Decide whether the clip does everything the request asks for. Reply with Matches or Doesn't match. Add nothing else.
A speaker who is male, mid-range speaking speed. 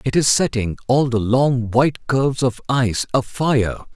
Matches